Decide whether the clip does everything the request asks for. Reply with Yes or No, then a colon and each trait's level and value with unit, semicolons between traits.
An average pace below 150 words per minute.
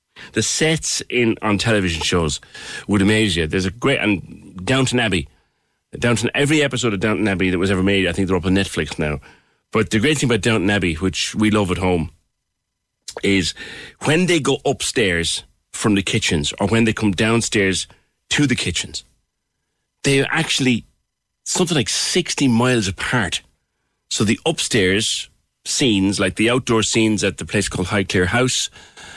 No: average, 165 wpm